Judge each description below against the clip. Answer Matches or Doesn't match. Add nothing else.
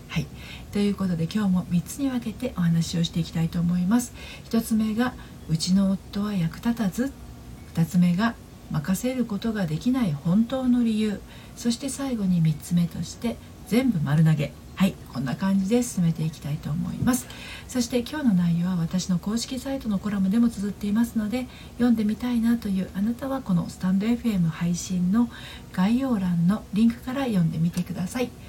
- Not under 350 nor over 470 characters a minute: Matches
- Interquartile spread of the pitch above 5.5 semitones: Doesn't match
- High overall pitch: Matches